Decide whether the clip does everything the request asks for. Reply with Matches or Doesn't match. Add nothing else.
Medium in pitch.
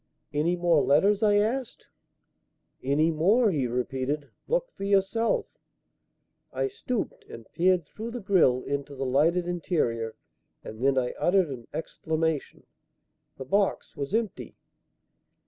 Matches